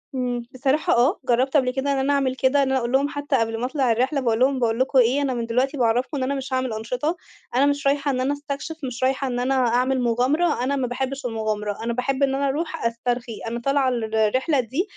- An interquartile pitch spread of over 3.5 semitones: No, narrow, 2.5 semitones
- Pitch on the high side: Yes, very high, 260 Hz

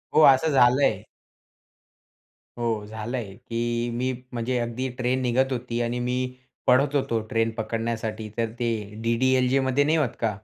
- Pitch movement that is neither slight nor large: No, narrow, 2.0 semitones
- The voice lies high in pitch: No, low, 120 Hz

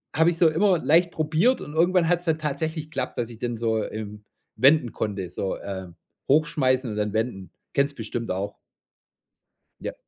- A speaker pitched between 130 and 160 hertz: Yes, low, 135 Hz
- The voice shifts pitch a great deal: Yes, wide, 6.7 semitones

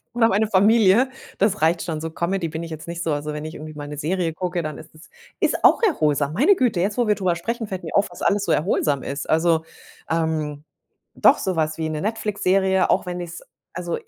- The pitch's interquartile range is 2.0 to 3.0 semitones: No, average, 3.9 semitones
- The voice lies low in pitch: No, medium, 170 Hz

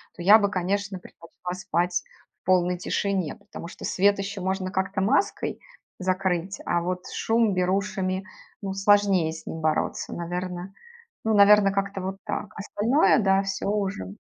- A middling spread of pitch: No, narrow, 1.9 semitones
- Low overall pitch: No, high, 190 Hz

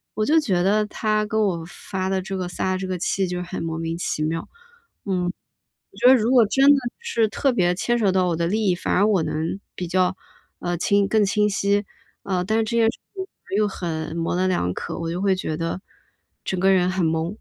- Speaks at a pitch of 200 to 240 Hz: No, high, 190 Hz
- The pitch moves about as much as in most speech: Yes, average, 3.2 semitones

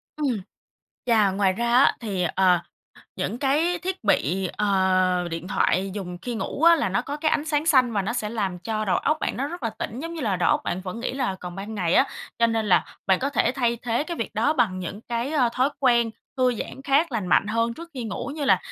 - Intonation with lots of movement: Yes, wide, 6.1 semitones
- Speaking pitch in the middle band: No, high, 230 Hz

